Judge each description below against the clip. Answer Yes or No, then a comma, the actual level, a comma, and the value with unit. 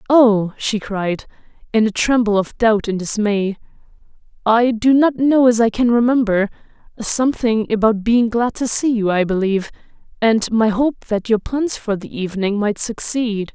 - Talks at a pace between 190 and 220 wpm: No, average, 170 wpm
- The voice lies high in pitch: Yes, high, 220 Hz